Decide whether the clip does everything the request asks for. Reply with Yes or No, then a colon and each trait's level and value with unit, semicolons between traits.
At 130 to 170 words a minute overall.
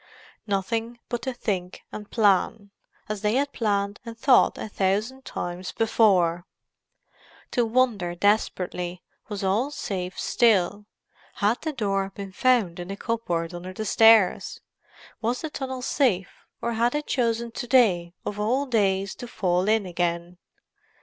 Yes: average, 145 wpm